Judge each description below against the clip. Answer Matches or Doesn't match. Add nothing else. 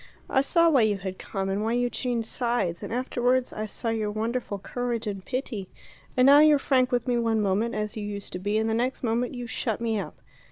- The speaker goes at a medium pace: Doesn't match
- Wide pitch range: Doesn't match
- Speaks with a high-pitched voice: Matches